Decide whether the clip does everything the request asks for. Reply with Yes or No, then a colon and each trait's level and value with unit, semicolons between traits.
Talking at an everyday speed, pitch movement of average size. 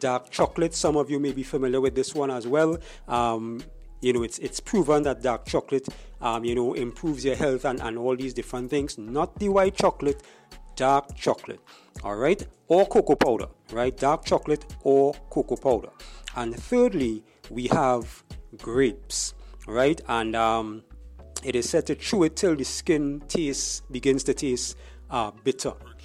Yes: average, 170 wpm; average, 3.5 semitones